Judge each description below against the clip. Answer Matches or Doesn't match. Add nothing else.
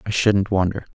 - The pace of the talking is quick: Doesn't match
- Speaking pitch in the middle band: Doesn't match